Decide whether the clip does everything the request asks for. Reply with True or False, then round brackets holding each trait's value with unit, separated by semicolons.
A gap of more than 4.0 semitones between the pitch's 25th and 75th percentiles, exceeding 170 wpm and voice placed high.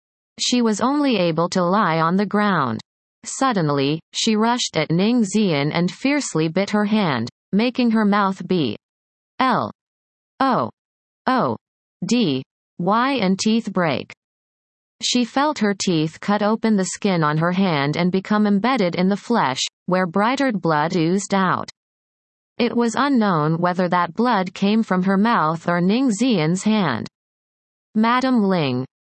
False (4.7 semitones; 145 wpm; 195 Hz)